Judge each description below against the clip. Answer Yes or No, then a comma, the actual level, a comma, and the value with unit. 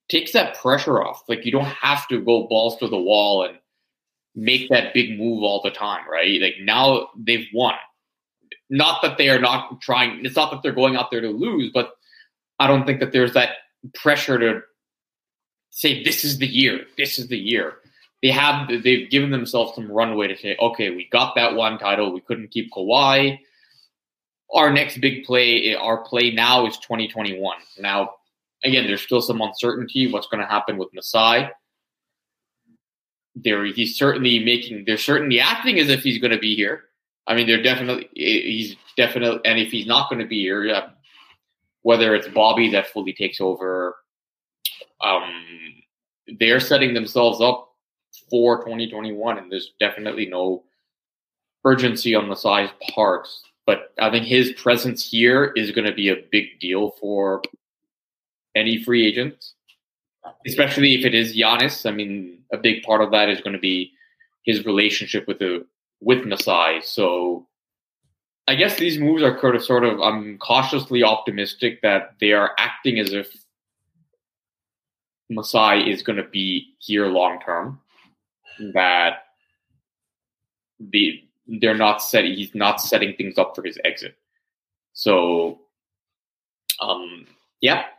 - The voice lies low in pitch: Yes, low, 115 Hz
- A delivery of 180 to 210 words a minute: No, average, 155 wpm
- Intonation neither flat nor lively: Yes, average, 3.5 semitones